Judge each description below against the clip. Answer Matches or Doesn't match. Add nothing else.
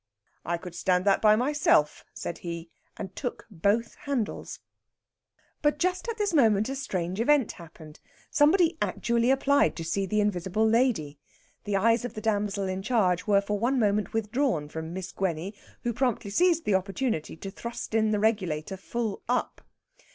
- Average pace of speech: Matches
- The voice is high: Matches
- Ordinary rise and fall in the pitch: Matches